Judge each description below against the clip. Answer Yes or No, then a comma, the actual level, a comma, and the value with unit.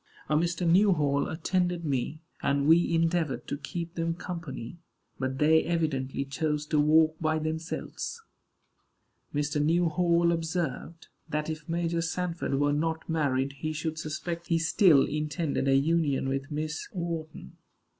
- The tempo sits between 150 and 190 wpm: No, slow, 135 wpm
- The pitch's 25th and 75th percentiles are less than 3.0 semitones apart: Yes, narrow, 2.4 semitones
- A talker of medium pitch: Yes, medium, 160 Hz